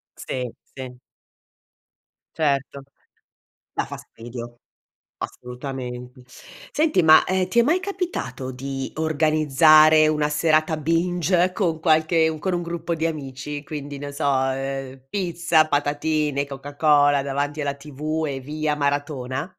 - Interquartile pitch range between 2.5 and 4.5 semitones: Yes, average, 2.8 semitones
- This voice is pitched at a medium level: Yes, medium, 150 Hz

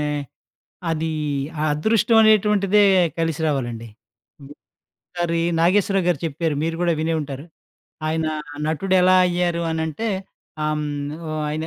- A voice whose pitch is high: No, medium, 165 Hz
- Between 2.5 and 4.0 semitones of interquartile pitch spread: Yes, average, 3.4 semitones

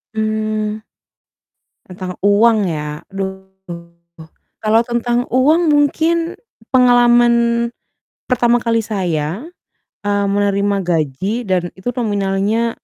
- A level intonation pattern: No, average, 3.7 semitones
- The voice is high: Yes, high, 215 Hz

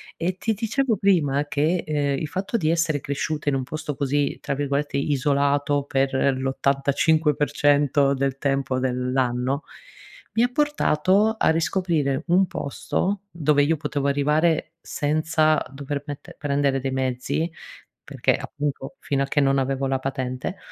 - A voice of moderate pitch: Yes, medium, 145 Hz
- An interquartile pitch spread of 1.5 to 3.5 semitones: Yes, average, 2.7 semitones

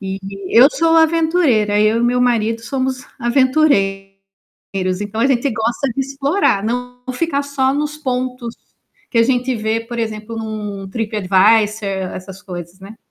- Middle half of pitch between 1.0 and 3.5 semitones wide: No, average, 4.2 semitones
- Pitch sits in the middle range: No, high, 230 Hz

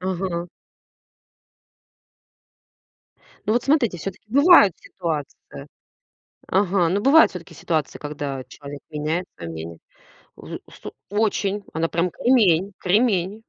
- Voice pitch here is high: No, medium, 180 Hz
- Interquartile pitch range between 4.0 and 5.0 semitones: Yes, average, 4.7 semitones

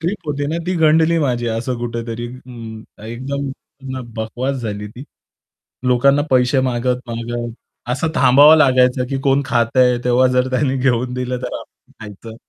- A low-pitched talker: Yes, low, 125 Hz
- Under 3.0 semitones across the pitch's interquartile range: Yes, narrow, 2.6 semitones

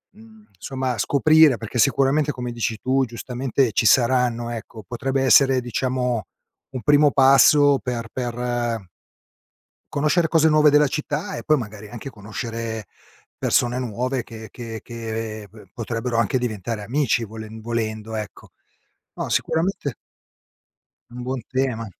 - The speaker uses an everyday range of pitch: Yes, average, 3.1 semitones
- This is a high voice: No, low, 125 Hz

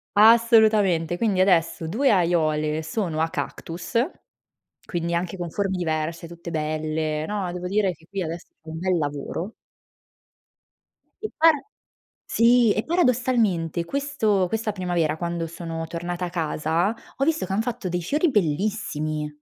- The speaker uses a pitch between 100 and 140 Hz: No, medium, 175 Hz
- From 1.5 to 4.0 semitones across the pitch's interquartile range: No, average, 4.7 semitones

